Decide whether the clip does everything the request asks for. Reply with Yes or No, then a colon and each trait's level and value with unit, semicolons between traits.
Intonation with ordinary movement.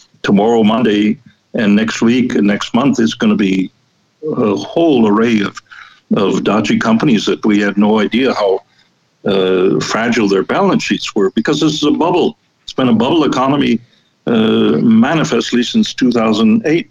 Yes: average, 3.3 semitones